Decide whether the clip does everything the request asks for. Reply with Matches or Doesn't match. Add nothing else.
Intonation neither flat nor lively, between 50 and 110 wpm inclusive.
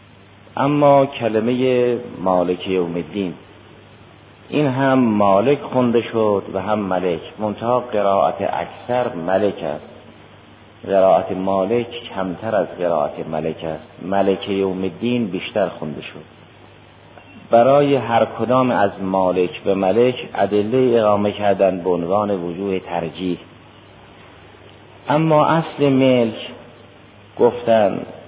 Matches